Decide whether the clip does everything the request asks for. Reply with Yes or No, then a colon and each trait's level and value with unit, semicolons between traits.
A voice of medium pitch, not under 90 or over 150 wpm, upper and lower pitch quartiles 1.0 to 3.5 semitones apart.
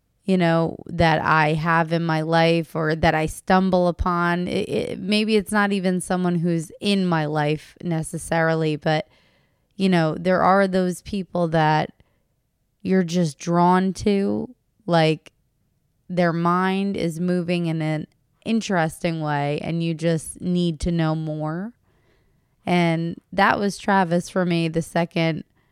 Yes: medium, 170 Hz; average, 140 wpm; narrow, 2.6 semitones